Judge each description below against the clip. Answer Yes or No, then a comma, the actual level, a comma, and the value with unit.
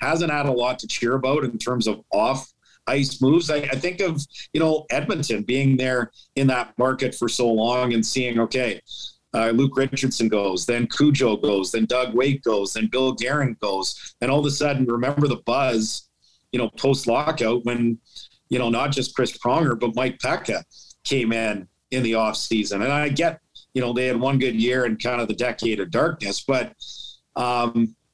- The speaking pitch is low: Yes, low, 125 Hz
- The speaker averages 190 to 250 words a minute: Yes, average, 200 wpm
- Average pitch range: Yes, average, 3.0 semitones